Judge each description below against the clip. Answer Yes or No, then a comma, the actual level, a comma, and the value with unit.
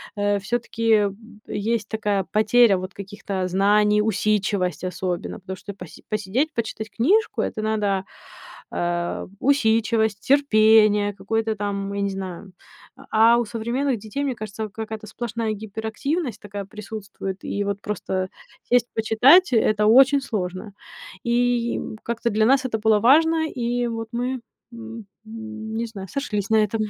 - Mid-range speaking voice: No, high, 220 Hz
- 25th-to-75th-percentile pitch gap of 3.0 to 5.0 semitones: No, narrow, 2.6 semitones